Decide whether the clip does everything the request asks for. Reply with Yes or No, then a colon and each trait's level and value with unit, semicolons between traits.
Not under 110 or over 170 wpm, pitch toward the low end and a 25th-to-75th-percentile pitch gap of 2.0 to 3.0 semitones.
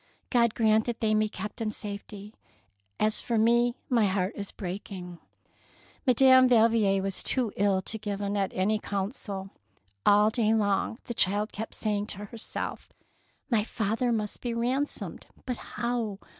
No: average, 155 wpm; high, 215 Hz; narrow, 2.5 semitones